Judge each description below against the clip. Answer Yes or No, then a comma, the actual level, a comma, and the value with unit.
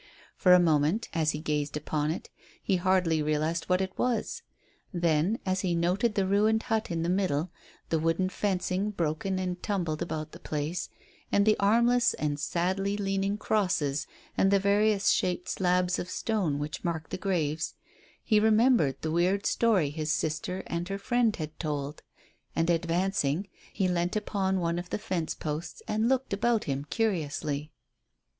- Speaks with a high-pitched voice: No, medium, 180 Hz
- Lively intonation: No, average, 4.2 semitones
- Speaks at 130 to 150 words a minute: No, average, 165 wpm